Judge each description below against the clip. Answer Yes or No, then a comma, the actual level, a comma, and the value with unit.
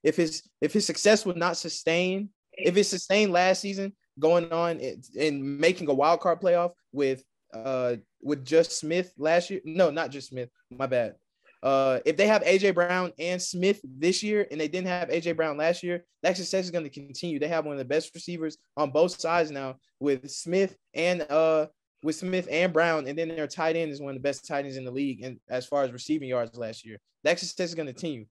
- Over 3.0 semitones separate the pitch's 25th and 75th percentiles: Yes, average, 4.1 semitones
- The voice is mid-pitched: Yes, medium, 165 Hz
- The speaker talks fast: Yes, fast, 225 wpm